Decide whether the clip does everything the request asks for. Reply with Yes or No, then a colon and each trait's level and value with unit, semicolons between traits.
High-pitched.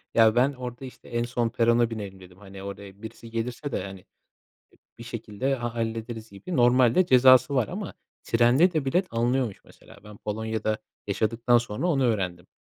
No: low, 115 Hz